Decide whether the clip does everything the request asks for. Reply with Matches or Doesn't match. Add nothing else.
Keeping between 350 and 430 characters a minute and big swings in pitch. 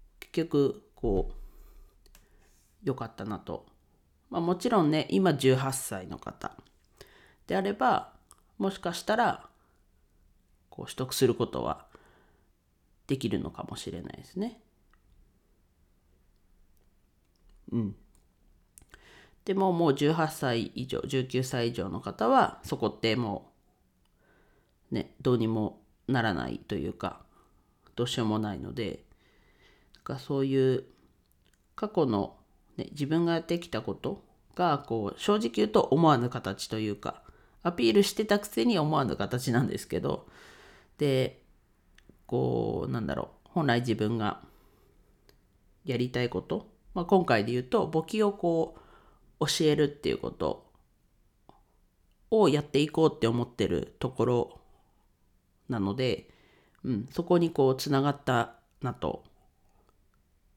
Doesn't match